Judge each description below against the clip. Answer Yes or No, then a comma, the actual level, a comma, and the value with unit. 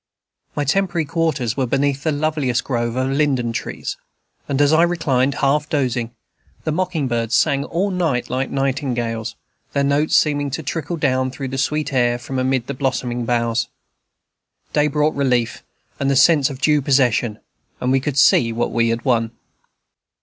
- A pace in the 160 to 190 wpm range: Yes, average, 170 wpm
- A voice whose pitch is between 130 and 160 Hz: Yes, low, 135 Hz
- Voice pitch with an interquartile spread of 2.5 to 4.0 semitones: Yes, average, 3.3 semitones